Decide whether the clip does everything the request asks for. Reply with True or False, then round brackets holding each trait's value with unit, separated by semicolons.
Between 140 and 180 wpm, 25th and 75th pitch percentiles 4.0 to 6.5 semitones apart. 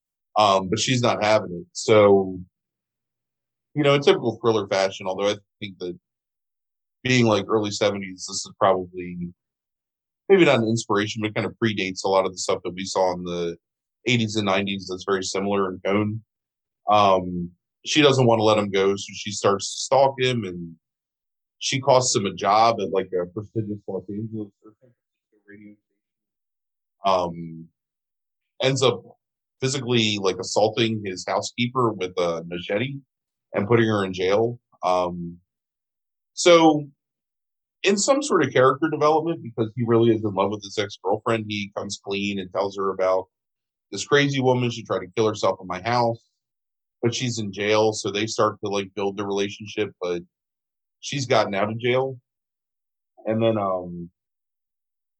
False (165 wpm; 3.4 semitones)